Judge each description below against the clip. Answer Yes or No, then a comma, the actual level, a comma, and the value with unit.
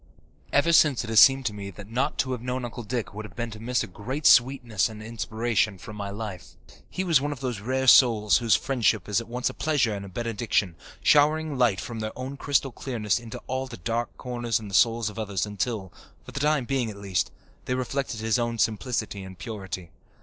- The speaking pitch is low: Yes, low, 115 Hz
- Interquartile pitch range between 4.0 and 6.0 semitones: No, average, 3.6 semitones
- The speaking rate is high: Yes, fast, 225 wpm